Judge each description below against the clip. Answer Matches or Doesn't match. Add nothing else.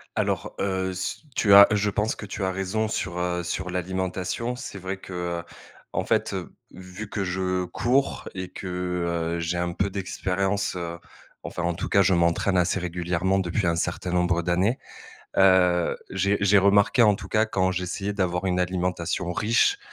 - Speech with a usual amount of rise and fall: Doesn't match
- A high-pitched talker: Doesn't match